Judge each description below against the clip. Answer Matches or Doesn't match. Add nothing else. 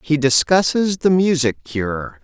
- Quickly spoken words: Doesn't match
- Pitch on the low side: Doesn't match